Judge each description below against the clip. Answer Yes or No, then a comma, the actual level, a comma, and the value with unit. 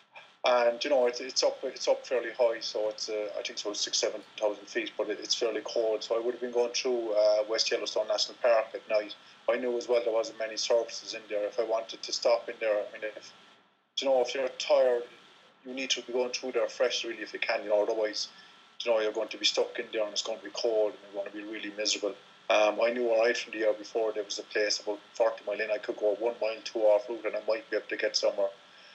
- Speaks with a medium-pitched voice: No, low, 110 Hz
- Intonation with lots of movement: No, narrow, 2.6 semitones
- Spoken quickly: Yes, fast, 280 wpm